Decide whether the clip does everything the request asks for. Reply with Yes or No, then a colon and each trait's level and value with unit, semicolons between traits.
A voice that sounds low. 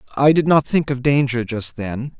Yes: low, 130 Hz